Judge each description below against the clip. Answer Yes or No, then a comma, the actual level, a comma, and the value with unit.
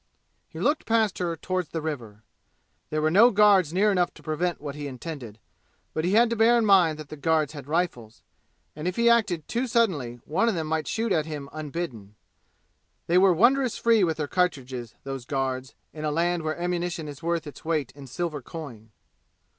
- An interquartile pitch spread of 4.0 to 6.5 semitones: Yes, average, 4.3 semitones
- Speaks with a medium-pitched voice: Yes, medium, 160 Hz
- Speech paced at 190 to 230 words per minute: Yes, average, 200 wpm